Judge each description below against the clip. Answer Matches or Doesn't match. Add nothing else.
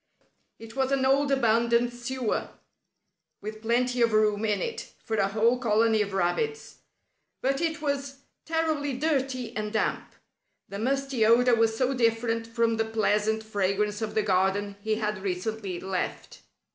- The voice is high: Matches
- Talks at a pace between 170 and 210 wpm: Doesn't match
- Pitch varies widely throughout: Doesn't match